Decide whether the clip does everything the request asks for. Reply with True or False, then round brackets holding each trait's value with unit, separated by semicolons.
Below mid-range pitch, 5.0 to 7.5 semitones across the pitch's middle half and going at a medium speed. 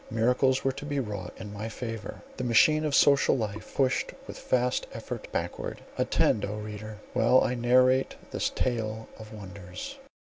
False (115 Hz; 3.3 semitones; 165 wpm)